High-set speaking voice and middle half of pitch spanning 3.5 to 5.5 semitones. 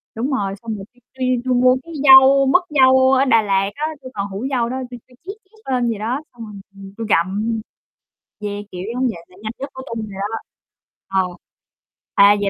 Yes: high, 235 Hz; average, 4.4 semitones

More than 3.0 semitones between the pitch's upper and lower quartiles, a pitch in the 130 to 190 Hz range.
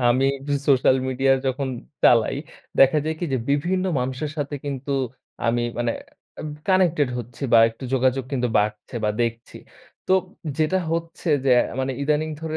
Yes: average, 3.6 semitones; low, 135 Hz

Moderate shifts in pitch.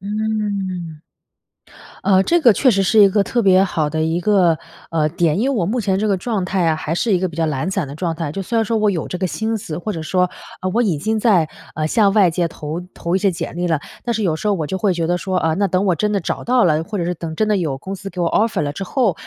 Yes: average, 4.0 semitones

